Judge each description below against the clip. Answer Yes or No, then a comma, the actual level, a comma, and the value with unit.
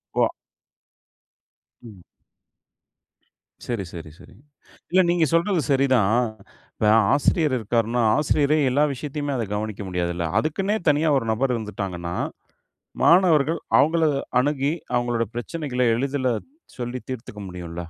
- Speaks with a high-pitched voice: No, low, 125 Hz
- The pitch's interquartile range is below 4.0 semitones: No, wide, 5.5 semitones